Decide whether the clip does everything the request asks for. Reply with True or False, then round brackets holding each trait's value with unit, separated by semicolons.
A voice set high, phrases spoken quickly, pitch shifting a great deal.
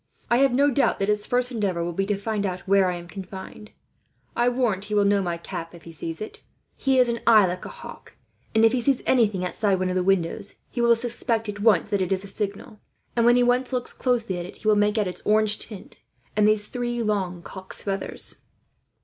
False (210 Hz; 240 wpm; 3.8 semitones)